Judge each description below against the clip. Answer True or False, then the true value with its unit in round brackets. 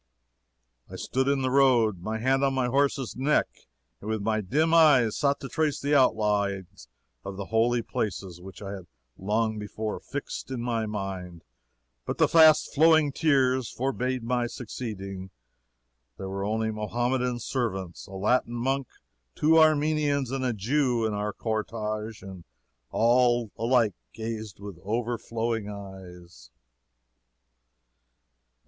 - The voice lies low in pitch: True (115 Hz)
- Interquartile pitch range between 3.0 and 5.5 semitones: True (4.3 semitones)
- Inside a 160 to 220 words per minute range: False (135 wpm)